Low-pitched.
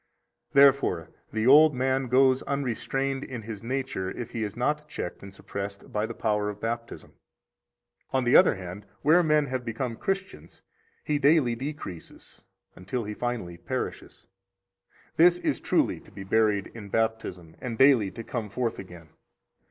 Yes: low, 120 Hz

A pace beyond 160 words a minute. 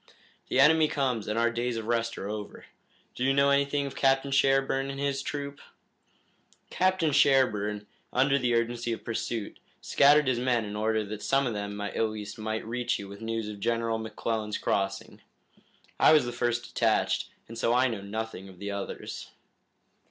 Yes: average, 180 wpm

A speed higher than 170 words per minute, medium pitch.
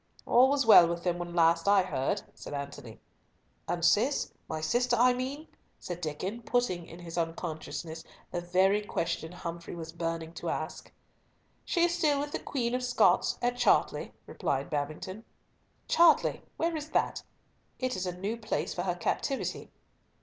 No: average, 160 wpm; medium, 180 Hz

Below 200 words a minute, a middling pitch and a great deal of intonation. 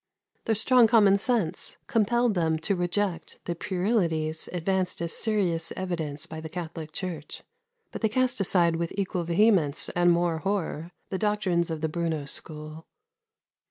No: average, 150 wpm; medium, 175 Hz; average, 3.9 semitones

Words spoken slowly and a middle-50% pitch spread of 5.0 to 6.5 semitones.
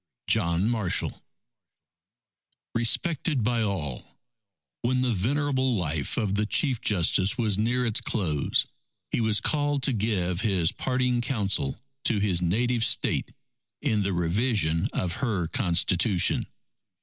Yes: slow, 125 wpm; average, 5.3 semitones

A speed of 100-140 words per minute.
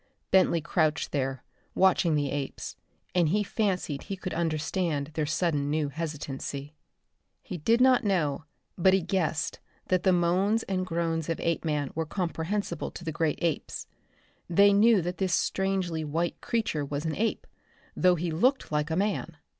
No: average, 160 wpm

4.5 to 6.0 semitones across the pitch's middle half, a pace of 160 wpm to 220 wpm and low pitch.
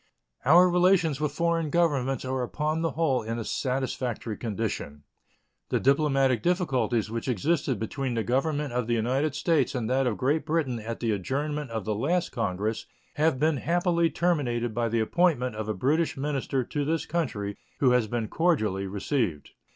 Yes: average, 5.3 semitones; average, 170 wpm; low, 130 Hz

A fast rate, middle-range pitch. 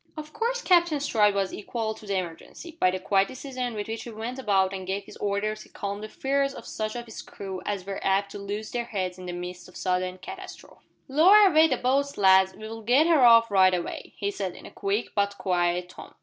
No: fast, 235 wpm; high, 205 Hz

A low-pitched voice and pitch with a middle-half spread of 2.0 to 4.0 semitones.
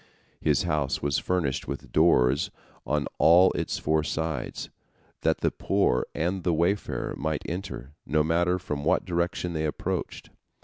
Yes: very low, 80 Hz; average, 3.1 semitones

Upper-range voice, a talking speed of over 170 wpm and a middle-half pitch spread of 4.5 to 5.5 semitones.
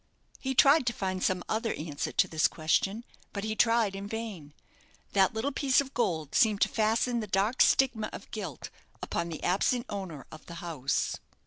Yes: high, 205 Hz; average, 185 wpm; average, 5.1 semitones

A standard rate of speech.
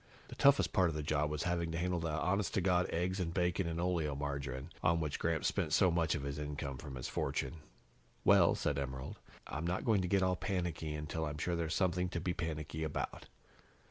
No: fast, 215 wpm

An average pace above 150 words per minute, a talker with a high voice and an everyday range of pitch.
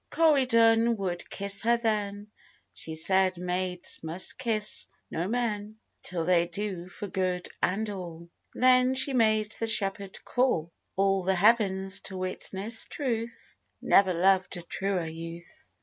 No: slow, 135 wpm; high, 195 Hz; average, 3.8 semitones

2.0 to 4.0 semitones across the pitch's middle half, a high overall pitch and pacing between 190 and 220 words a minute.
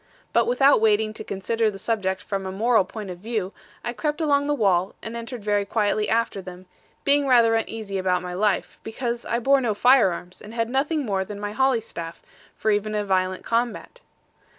Yes: average, 3.5 semitones; high, 215 Hz; average, 200 wpm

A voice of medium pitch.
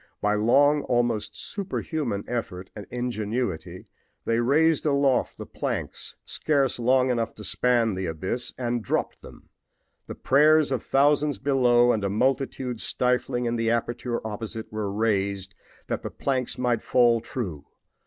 No: low, 120 Hz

